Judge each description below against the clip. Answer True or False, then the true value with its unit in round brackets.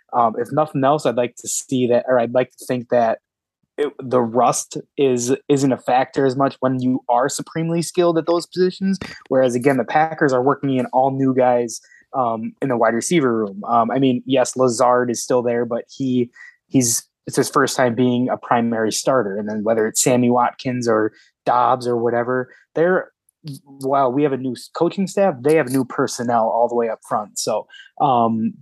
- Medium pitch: False (125 Hz)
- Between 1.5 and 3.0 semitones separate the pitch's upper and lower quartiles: True (2.5 semitones)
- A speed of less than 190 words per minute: False (200 wpm)